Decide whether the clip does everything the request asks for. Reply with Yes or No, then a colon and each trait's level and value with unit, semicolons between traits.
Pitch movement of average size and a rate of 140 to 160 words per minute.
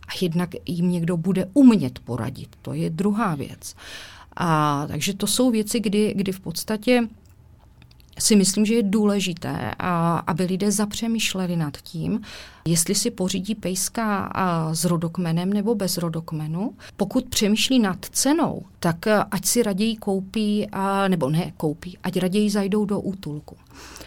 Yes: average, 3.9 semitones; average, 145 wpm